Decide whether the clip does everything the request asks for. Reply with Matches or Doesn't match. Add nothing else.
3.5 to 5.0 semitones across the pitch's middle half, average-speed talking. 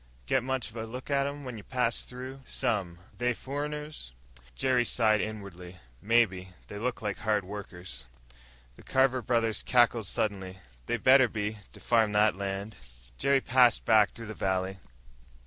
Matches